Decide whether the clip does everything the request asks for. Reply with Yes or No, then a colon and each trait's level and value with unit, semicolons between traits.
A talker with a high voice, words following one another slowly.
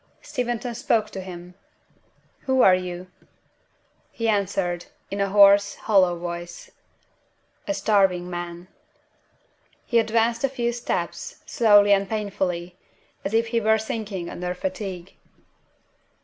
Yes: high, 200 Hz; slow, 120 wpm